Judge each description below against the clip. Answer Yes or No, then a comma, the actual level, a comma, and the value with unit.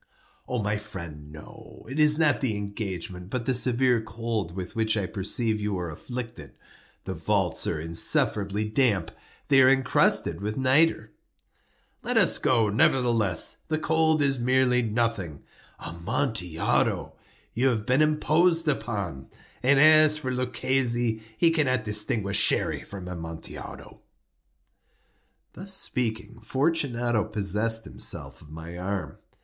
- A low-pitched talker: Yes, low, 115 Hz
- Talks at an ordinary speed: No, slow, 125 wpm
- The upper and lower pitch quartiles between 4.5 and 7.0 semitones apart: Yes, average, 4.9 semitones